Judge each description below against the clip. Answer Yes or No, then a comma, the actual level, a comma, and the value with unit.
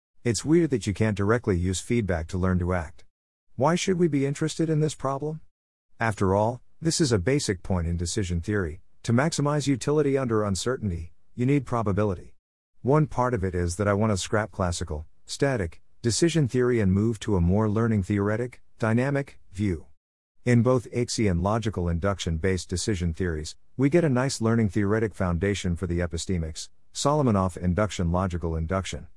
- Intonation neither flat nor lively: No, wide, 5.7 semitones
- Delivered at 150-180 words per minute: Yes, average, 170 wpm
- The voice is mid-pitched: No, low, 105 Hz